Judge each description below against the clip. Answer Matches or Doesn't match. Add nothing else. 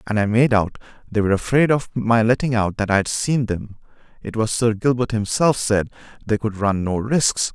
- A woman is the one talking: Doesn't match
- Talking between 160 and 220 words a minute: Matches